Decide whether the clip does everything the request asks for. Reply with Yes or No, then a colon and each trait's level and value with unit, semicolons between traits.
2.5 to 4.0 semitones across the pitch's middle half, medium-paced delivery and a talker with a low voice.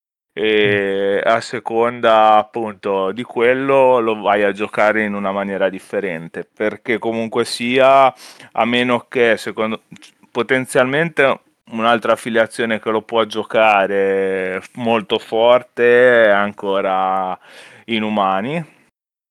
No: average, 3.1 semitones; slow, 105 wpm; low, 110 Hz